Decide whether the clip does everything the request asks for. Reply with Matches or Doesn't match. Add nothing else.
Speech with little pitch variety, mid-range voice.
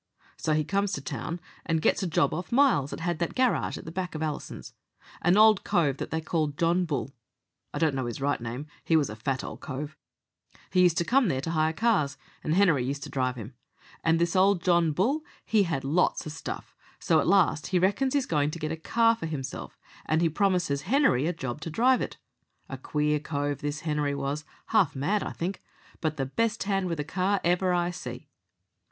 Doesn't match